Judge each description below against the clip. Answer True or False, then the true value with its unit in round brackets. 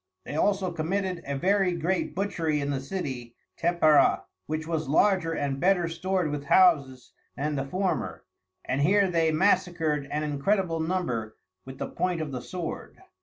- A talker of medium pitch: True (165 Hz)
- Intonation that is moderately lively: True (4.4 semitones)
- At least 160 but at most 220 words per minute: True (165 wpm)